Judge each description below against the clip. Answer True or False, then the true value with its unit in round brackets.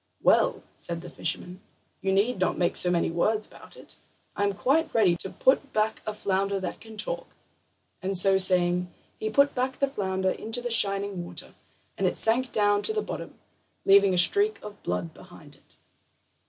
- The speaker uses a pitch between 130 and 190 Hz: False (200 Hz)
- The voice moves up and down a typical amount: True (3.5 semitones)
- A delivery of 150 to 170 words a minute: False (185 wpm)